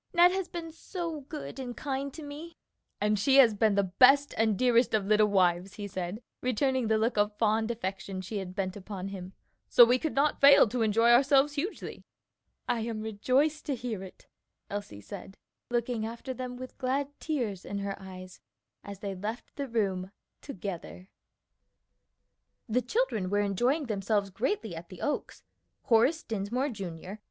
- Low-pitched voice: No, high, 225 Hz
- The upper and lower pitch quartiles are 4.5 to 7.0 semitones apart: Yes, average, 5.1 semitones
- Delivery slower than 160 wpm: No, average, 170 wpm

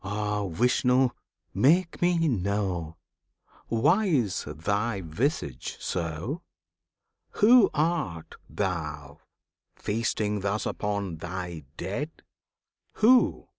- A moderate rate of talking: No, slow, 85 wpm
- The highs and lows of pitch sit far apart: Yes, wide, 8.5 semitones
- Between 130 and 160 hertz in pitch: No, low, 105 Hz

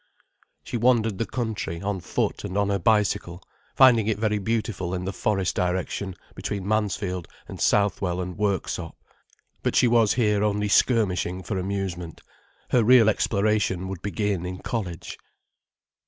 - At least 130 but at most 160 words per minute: Yes, average, 145 wpm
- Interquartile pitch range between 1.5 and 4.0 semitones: Yes, average, 2.9 semitones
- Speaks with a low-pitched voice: Yes, low, 100 Hz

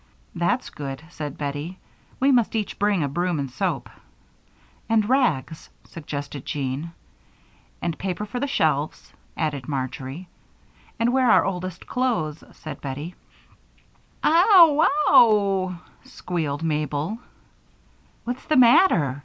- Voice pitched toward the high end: No, medium, 170 Hz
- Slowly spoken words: Yes, slow, 120 wpm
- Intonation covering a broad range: Yes, wide, 7.7 semitones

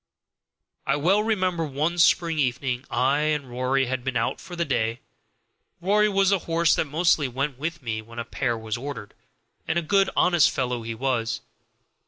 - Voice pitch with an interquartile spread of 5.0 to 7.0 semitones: Yes, wide, 5.6 semitones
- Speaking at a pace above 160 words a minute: Yes, average, 180 wpm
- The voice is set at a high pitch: No, medium, 140 Hz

